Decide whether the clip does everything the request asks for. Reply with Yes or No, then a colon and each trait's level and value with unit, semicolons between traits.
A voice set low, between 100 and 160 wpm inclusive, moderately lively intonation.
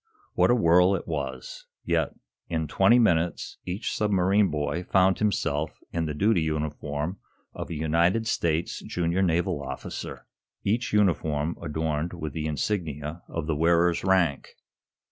Yes: very low, 85 Hz; average, 140 wpm; average, 3.5 semitones